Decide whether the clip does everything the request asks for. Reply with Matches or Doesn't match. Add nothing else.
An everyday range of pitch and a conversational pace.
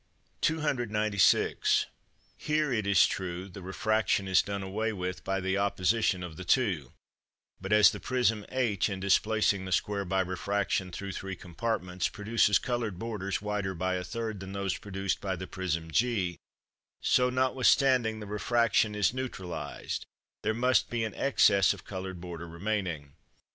Matches